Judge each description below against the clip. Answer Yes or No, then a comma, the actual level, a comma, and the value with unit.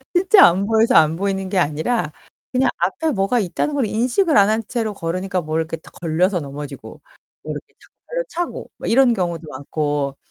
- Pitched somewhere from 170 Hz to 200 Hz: Yes, high, 190 Hz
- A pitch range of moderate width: No, wide, 6.7 semitones